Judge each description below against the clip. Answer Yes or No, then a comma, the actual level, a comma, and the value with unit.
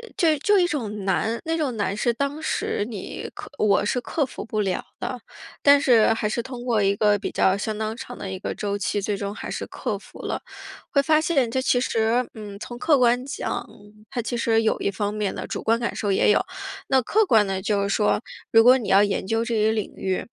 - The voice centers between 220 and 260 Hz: Yes, high, 225 Hz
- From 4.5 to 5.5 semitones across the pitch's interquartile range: No, average, 3.7 semitones